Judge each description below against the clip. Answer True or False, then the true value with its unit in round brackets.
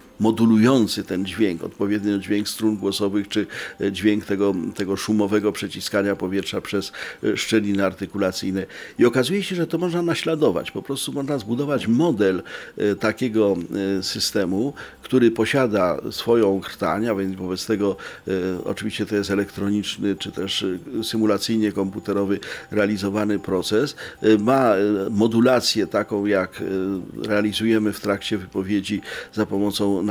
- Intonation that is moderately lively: False (1.9 semitones)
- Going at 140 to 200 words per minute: False (120 wpm)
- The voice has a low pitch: True (105 Hz)